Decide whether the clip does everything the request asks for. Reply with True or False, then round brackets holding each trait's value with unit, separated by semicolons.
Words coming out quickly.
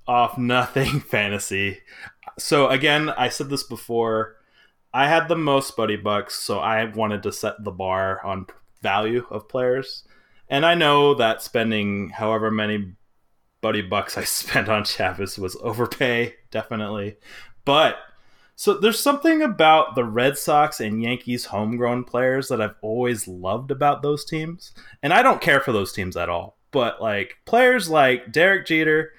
False (155 wpm)